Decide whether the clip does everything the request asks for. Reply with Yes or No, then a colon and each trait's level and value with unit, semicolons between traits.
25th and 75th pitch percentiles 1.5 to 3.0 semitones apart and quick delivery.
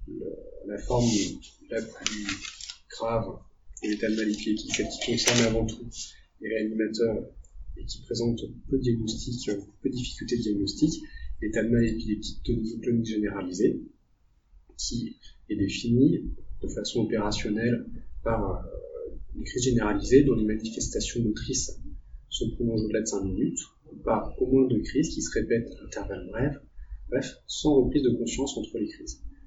No: narrow, 2.6 semitones; average, 155 wpm